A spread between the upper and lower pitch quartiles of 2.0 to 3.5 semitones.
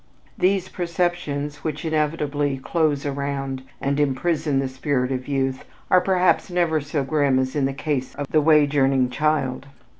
Yes: narrow, 2.6 semitones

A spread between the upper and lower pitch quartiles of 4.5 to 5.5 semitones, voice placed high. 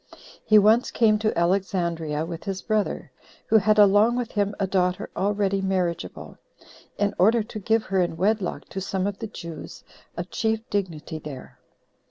No: average, 3.1 semitones; high, 195 Hz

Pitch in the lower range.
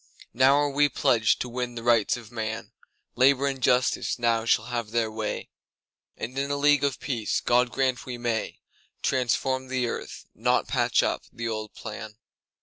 Yes: low, 120 Hz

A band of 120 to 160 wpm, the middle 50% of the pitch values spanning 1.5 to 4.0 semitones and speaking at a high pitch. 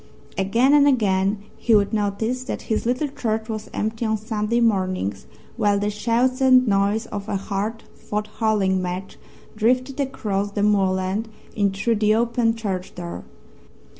Yes: average, 155 wpm; average, 2.8 semitones; high, 215 Hz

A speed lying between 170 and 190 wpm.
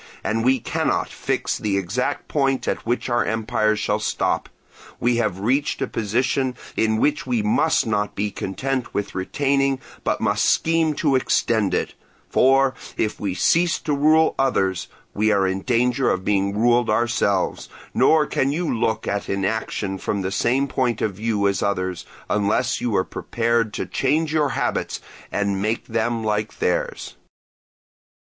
No: average, 160 wpm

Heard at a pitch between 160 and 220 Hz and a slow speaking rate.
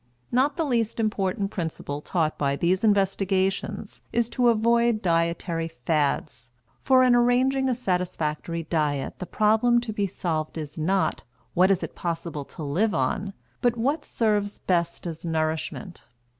No: high, 190 Hz; average, 145 wpm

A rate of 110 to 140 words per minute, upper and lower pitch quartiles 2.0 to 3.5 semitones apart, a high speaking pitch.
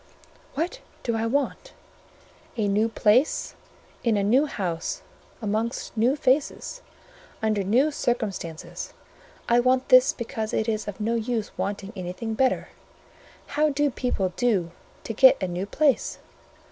No: slow, 135 wpm; average, 4.1 semitones; high, 230 Hz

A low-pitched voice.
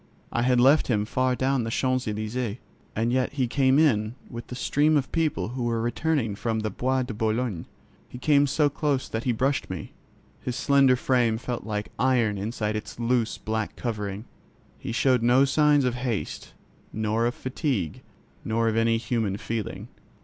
Yes: low, 120 Hz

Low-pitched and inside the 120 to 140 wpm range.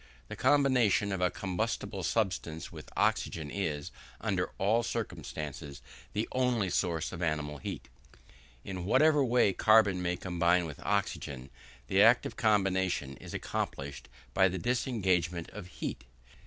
Yes: very low, 95 Hz; slow, 135 wpm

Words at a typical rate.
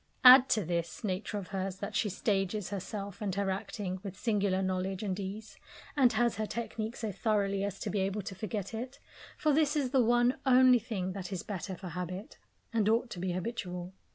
No: fast, 210 wpm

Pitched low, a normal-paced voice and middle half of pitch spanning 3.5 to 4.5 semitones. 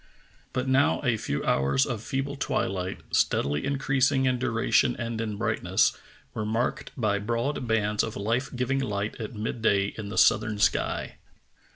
Yes: low, 115 Hz; average, 165 wpm; average, 3.8 semitones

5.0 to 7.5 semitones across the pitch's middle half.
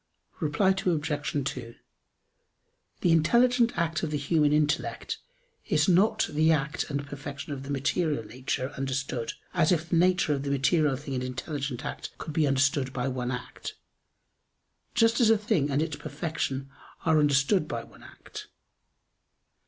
No: average, 3.3 semitones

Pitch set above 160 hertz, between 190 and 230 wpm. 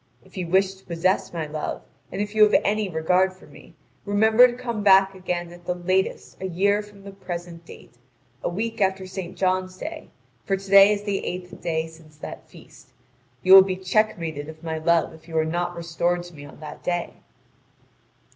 Yes: medium, 185 Hz; fast, 205 wpm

